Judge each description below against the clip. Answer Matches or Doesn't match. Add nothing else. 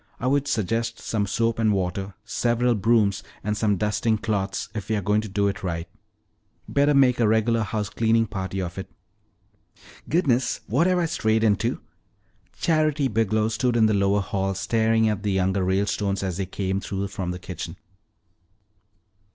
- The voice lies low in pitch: Matches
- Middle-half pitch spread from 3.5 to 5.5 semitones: Doesn't match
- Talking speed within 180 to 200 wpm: Doesn't match